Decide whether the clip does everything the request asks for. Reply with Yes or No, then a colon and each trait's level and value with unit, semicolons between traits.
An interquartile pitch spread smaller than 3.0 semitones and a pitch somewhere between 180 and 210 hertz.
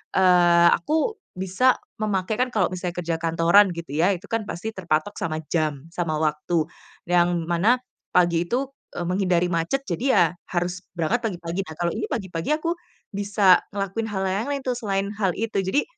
No: average, 3.4 semitones; medium, 185 Hz